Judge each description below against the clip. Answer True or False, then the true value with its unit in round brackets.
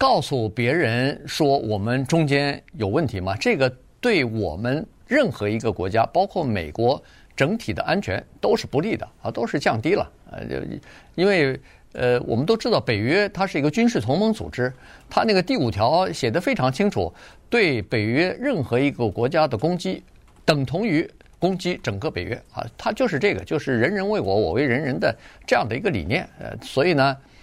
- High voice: False (135 Hz)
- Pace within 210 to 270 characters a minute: False (280 characters per minute)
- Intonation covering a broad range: True (6.9 semitones)